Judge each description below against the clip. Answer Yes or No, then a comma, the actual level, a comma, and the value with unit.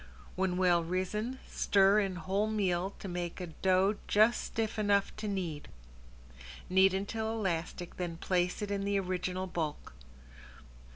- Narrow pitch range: Yes, narrow, 2.3 semitones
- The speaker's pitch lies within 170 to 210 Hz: Yes, high, 190 Hz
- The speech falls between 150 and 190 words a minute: No, average, 140 wpm